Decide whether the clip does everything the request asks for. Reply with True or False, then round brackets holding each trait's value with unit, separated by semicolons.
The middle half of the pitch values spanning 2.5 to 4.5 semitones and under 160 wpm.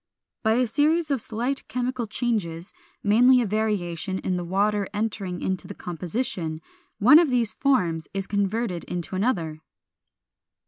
False (5.3 semitones; 140 wpm)